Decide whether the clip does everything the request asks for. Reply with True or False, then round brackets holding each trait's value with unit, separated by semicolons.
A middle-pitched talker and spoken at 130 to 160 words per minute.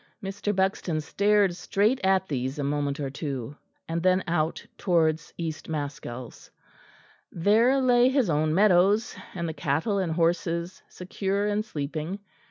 True (175 Hz; 140 wpm)